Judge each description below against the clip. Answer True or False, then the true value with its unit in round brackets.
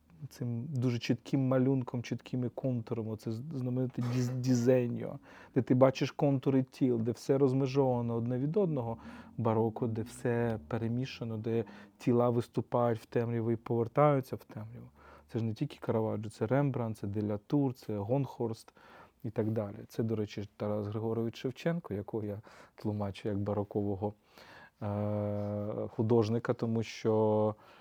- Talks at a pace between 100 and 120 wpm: False (135 wpm)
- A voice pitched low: True (115 Hz)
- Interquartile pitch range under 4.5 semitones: True (2.9 semitones)